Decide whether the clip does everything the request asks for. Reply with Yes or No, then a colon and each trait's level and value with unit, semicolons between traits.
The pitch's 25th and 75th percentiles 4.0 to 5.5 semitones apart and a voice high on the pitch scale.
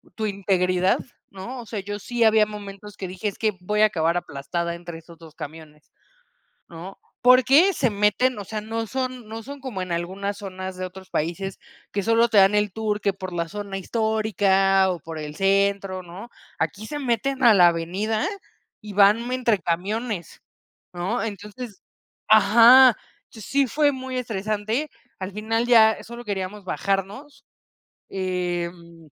No: average, 3.5 semitones; high, 205 Hz